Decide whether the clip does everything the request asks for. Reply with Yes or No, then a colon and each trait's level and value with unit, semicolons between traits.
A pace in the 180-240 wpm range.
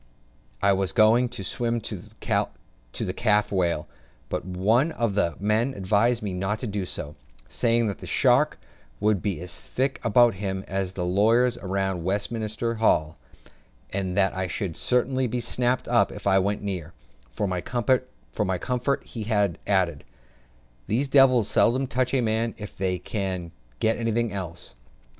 No: average, 155 wpm